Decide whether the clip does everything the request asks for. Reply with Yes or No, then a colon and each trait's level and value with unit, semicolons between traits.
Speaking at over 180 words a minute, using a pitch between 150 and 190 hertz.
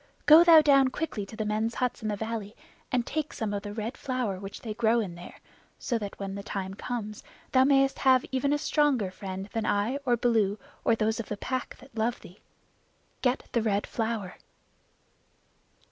No: average, 190 wpm; high, 225 Hz